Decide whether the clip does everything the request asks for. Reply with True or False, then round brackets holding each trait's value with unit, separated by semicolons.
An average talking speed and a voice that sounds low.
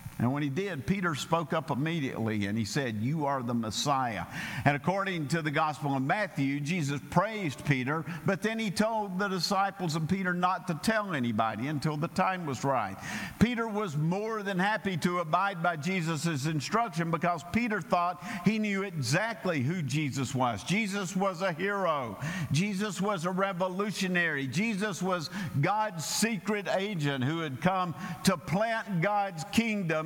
False (160 wpm; 175 Hz)